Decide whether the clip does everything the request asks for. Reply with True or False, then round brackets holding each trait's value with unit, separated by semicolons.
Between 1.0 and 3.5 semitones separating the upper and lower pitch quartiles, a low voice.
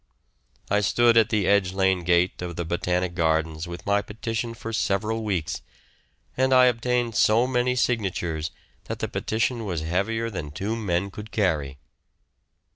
False (4.6 semitones; 100 Hz)